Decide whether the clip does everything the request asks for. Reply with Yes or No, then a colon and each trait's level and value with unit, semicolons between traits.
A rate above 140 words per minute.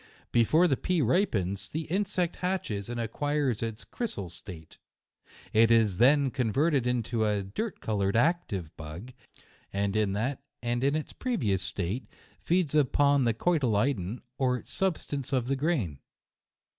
No: slow, 135 wpm